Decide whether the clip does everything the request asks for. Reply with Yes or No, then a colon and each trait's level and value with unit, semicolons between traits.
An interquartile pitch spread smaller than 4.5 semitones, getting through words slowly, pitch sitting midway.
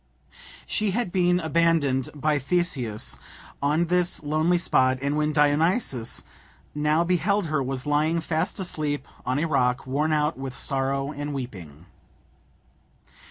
Yes: average, 3.7 semitones; slow, 130 wpm; medium, 150 Hz